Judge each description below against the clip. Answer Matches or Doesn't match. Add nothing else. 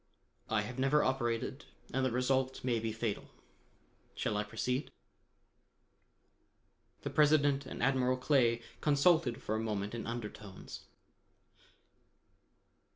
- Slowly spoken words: Matches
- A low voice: Matches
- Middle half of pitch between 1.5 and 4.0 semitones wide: Matches